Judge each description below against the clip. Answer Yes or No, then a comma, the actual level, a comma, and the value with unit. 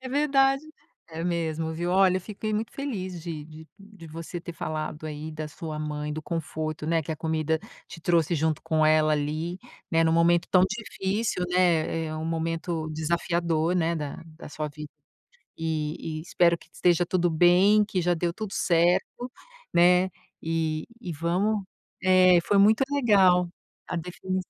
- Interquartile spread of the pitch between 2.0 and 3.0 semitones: Yes, average, 2.7 semitones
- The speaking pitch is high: No, medium, 170 Hz